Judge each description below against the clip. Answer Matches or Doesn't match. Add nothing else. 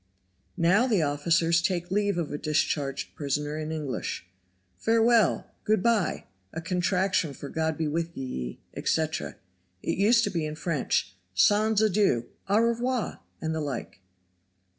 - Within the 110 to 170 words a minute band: Matches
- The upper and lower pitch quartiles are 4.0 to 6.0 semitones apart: Matches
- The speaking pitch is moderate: Matches